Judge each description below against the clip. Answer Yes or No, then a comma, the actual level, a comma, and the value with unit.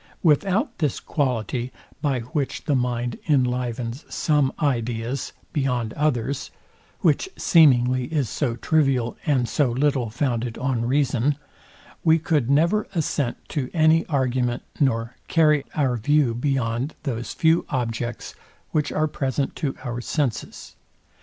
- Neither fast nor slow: No, slow, 125 wpm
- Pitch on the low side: Yes, low, 130 Hz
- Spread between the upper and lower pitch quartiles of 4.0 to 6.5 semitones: No, average, 3.5 semitones